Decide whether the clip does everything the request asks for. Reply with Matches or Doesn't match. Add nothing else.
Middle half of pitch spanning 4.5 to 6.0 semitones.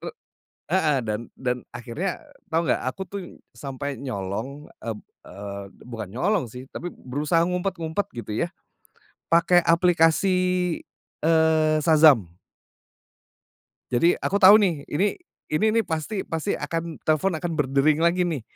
Matches